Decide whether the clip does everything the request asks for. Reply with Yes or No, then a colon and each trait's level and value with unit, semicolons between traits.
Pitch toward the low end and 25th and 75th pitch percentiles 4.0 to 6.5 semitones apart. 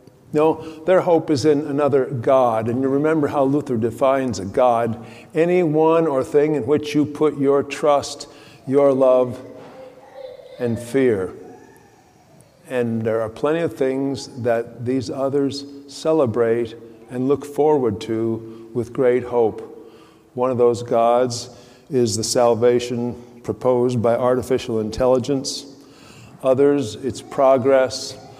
No: low, 130 Hz; average, 3.1 semitones